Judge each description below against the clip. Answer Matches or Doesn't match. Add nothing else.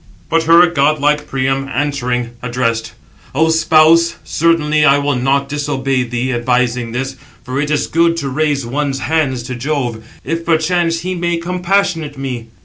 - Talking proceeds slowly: Doesn't match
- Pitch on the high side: Doesn't match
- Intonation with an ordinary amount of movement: Matches